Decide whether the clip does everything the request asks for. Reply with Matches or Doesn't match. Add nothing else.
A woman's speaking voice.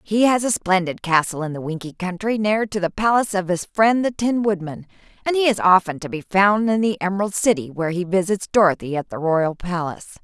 Matches